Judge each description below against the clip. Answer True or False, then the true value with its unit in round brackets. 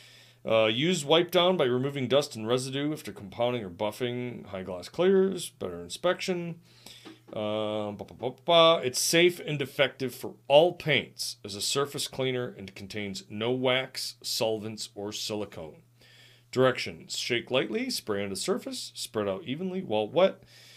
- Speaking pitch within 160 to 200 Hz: False (125 Hz)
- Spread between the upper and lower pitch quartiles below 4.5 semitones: False (5.2 semitones)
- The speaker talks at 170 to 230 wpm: False (140 wpm)